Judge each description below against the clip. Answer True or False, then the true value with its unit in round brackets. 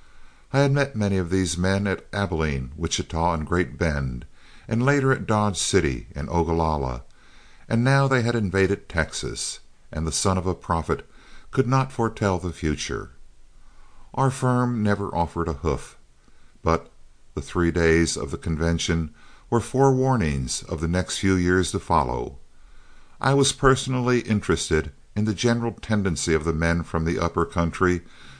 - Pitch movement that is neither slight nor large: False (5.9 semitones)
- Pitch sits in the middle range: False (90 Hz)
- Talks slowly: False (155 wpm)